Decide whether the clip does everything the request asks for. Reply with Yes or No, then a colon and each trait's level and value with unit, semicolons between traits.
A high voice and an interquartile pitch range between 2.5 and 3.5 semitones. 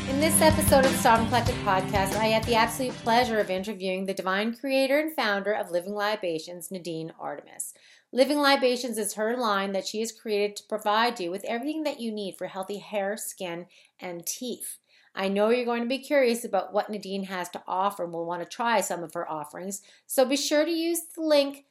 No: high, 210 Hz; average, 4.8 semitones